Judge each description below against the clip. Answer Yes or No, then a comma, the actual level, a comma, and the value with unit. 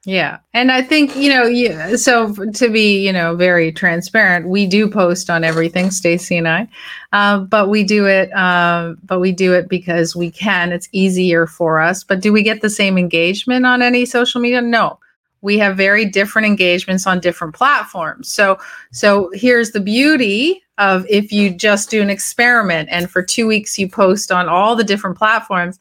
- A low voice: No, high, 200 Hz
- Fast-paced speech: No, average, 195 wpm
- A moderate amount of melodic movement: Yes, average, 3.4 semitones